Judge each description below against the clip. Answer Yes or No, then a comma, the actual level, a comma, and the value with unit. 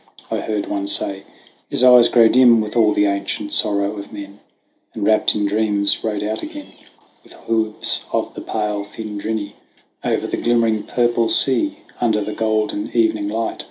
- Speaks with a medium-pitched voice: No, low, 110 Hz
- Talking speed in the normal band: Yes, average, 165 wpm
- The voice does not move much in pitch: Yes, narrow, 2.0 semitones